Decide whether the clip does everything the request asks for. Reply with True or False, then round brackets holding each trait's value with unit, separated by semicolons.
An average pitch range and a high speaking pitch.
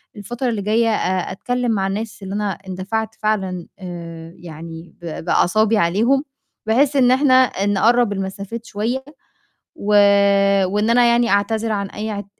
True (3.5 semitones; 210 Hz)